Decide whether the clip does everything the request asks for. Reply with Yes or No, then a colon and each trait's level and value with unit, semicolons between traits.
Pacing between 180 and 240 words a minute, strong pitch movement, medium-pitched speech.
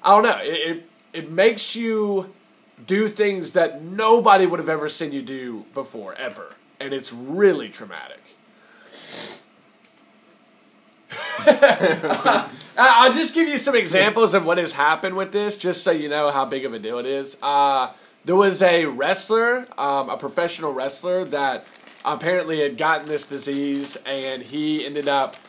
No: average, 160 wpm; wide, 6.4 semitones; medium, 165 Hz